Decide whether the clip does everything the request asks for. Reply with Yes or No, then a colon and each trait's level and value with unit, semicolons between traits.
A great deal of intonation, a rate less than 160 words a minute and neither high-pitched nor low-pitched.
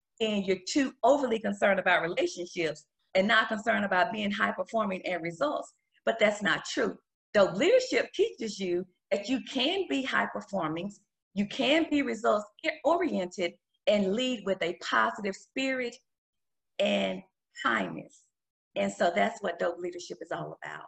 No: wide, 6.1 semitones; average, 150 wpm; high, 205 Hz